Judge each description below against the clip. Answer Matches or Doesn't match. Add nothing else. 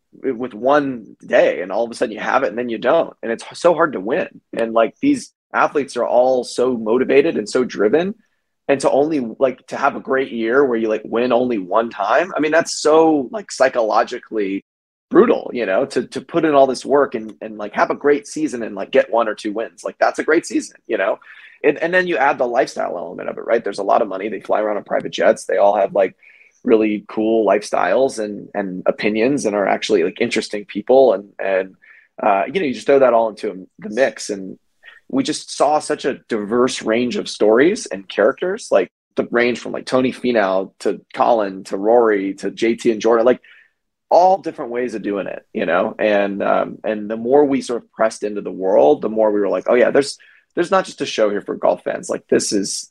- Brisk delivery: Matches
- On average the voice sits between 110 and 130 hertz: Matches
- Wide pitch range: Matches